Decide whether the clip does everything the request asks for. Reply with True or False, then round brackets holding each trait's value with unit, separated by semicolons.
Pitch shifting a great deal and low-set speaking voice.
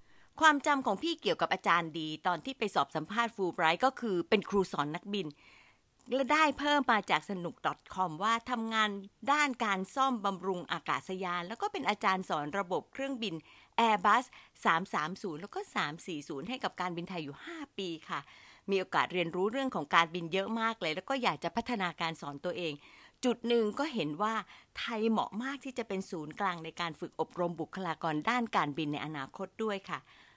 False (6.0 semitones; 195 Hz)